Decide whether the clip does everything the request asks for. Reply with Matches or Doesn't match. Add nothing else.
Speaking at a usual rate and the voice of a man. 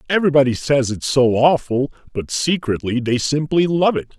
Matches